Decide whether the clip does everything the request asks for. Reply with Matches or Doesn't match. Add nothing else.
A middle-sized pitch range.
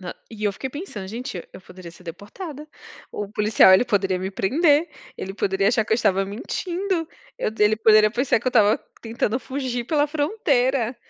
Doesn't match